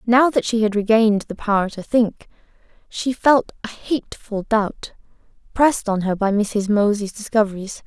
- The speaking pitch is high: Yes, high, 215 Hz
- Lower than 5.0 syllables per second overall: Yes, 4.8 syllables/s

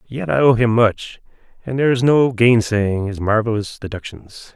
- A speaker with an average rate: Yes, average, 170 wpm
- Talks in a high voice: No, low, 115 Hz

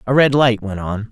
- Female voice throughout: No, male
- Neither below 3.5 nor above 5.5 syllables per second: Yes, 5.1 syllables/s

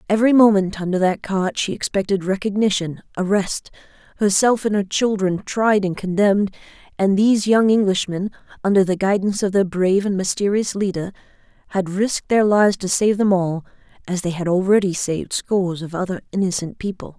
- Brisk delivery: No, average, 165 wpm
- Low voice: No, high, 195 Hz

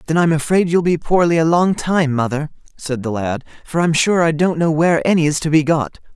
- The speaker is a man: Yes, male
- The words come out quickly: Yes, fast, 245 wpm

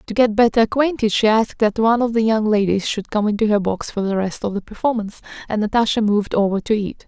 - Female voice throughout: Yes, female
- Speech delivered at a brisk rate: Yes, fast, 245 wpm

